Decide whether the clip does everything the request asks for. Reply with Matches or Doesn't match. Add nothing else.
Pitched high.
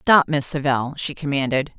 Doesn't match